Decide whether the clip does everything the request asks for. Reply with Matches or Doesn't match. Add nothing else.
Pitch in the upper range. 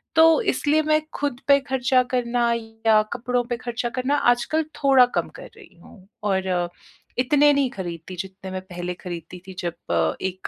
Matches